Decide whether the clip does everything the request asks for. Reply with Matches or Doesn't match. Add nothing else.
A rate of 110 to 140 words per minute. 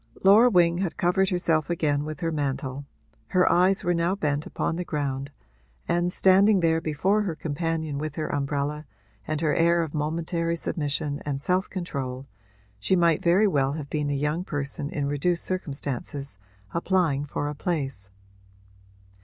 Doesn't match